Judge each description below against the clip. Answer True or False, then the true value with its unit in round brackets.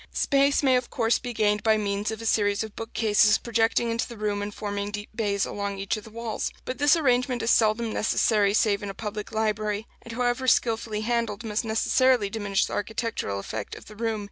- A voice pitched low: False (220 Hz)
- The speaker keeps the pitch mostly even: True (2.1 semitones)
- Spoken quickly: True (210 wpm)